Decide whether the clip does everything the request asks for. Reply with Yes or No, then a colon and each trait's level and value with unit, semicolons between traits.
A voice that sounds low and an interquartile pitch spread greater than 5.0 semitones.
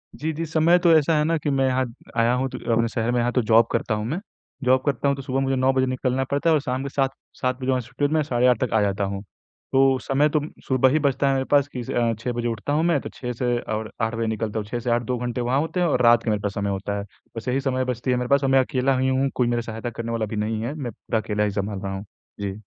No: low, 125 Hz; average, 3.1 semitones